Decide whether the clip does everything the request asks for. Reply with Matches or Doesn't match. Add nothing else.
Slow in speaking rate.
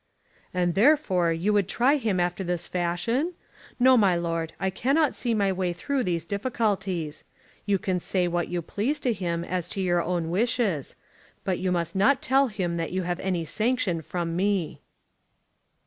Doesn't match